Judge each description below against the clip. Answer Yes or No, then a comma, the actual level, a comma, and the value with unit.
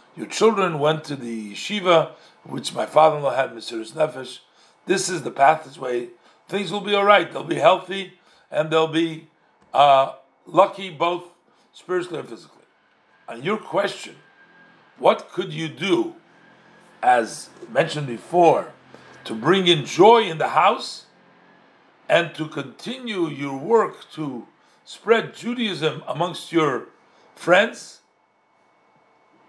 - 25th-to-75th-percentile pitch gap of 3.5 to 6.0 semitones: Yes, average, 4.2 semitones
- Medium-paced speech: No, slow, 130 wpm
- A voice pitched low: No, medium, 165 Hz